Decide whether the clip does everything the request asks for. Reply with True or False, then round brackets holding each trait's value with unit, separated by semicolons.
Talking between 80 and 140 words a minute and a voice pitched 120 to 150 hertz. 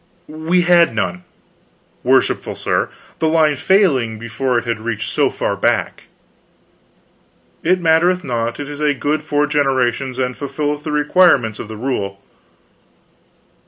True (135 wpm; 140 Hz)